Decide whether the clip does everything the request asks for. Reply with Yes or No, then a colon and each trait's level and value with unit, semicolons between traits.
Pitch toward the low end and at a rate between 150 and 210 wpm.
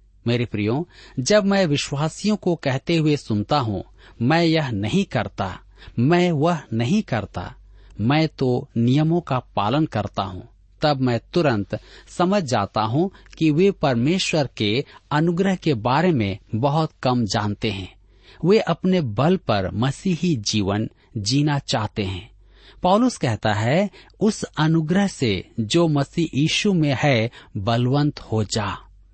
No: low, 130 Hz; average, 135 wpm